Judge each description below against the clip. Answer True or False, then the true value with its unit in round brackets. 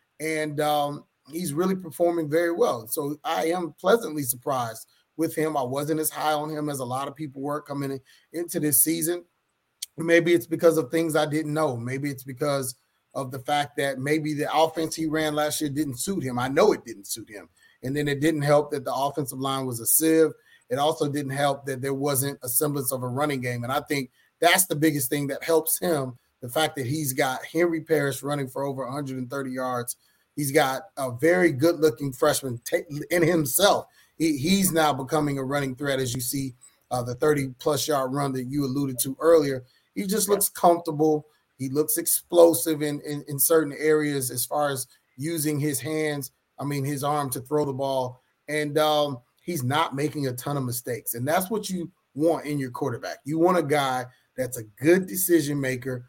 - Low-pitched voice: False (150 Hz)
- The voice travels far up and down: False (2.8 semitones)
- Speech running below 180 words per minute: False (200 wpm)